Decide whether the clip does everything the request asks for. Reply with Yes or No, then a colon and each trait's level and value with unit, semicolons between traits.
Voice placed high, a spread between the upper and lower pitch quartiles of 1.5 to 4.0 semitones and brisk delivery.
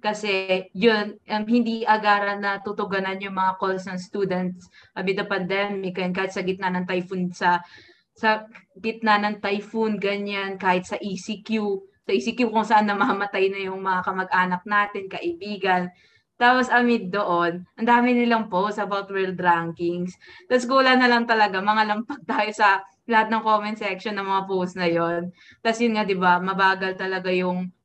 Yes: high, 200 Hz; narrow, 2.5 semitones; fast, 165 wpm